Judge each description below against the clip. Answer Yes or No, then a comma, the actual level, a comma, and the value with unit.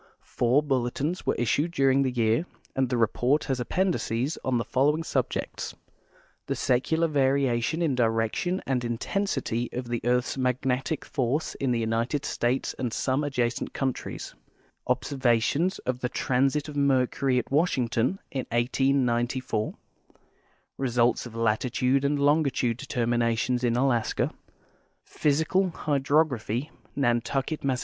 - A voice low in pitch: Yes, low, 130 Hz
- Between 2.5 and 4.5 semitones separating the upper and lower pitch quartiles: Yes, average, 2.9 semitones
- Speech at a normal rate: No, slow, 130 wpm